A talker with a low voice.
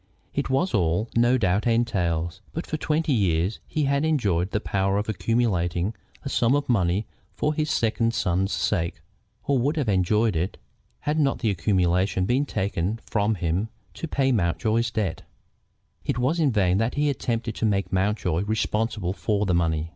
Yes: low, 105 Hz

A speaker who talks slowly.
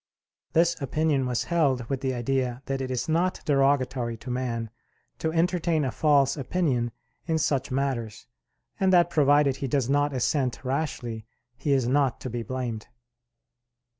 No: average, 155 wpm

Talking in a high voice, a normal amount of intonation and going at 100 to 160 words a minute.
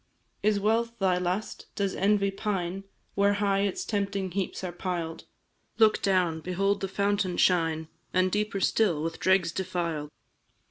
No: high, 195 Hz; narrow, 2.2 semitones; average, 145 wpm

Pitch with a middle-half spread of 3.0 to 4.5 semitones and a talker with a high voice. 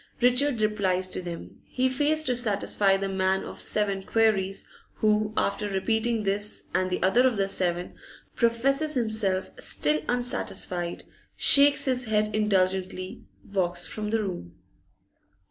Yes: average, 4.0 semitones; high, 210 Hz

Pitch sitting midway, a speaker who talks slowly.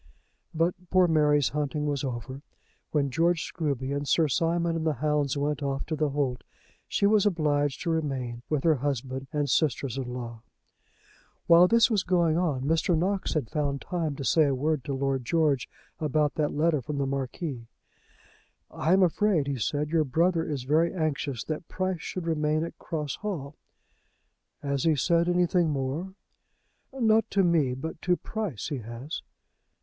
No: medium, 150 Hz; average, 170 wpm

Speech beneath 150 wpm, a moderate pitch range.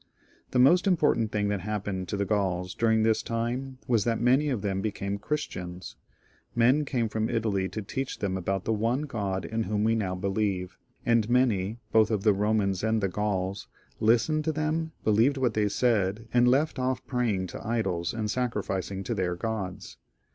No: average, 185 wpm; average, 3.8 semitones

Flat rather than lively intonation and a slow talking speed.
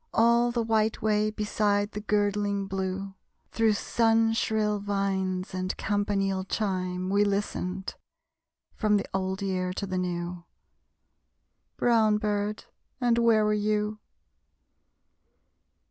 Yes: narrow, 1.9 semitones; slow, 115 wpm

